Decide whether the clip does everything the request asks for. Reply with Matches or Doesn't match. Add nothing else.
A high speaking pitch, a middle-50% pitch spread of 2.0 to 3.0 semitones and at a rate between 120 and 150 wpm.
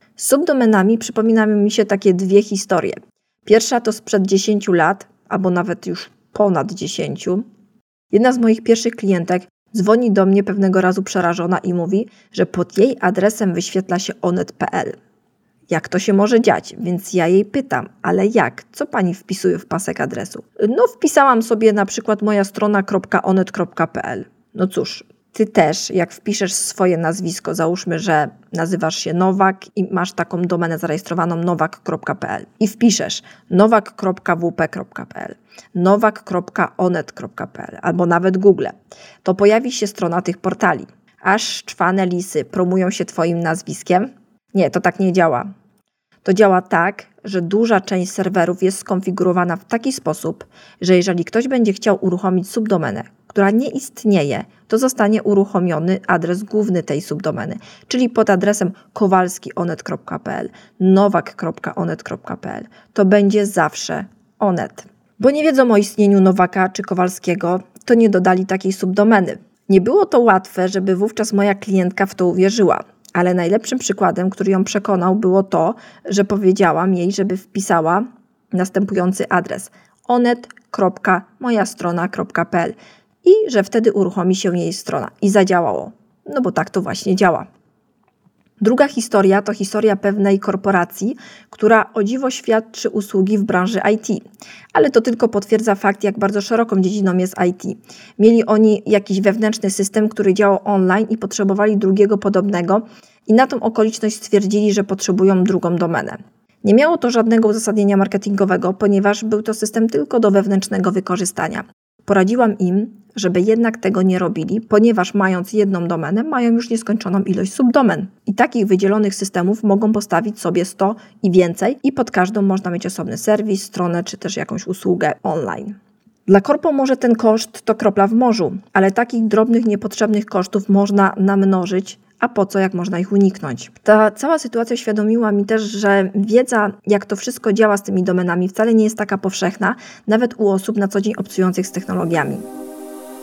Matches